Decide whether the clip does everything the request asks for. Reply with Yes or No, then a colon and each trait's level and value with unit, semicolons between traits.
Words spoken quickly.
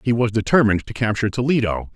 No: average, 185 wpm